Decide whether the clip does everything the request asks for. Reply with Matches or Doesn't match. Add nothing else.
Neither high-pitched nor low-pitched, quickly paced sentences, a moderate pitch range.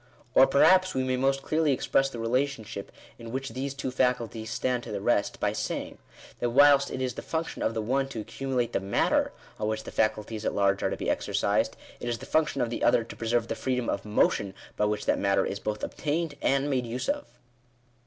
Doesn't match